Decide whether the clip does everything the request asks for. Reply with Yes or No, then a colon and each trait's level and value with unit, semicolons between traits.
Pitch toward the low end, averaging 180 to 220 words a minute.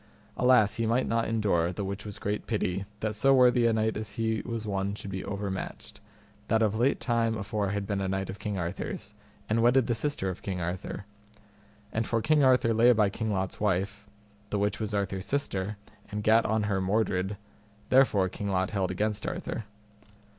Yes: low, 105 Hz; average, 195 wpm